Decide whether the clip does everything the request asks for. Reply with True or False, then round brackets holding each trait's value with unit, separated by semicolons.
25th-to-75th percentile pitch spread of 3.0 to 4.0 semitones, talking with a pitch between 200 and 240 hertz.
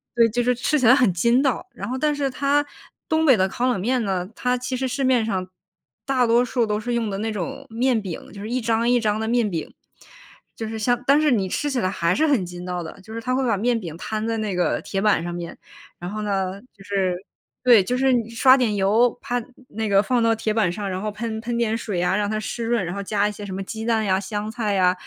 True (3.7 semitones; 220 Hz)